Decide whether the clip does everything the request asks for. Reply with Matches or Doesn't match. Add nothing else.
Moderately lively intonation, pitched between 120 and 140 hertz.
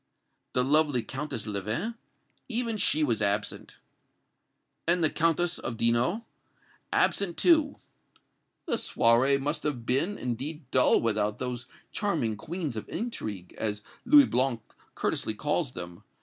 Doesn't match